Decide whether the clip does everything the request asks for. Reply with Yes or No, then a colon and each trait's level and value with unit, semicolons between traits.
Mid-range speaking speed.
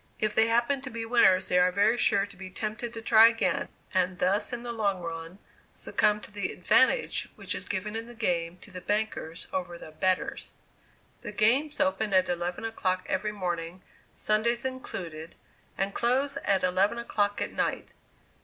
Yes: average, 180 wpm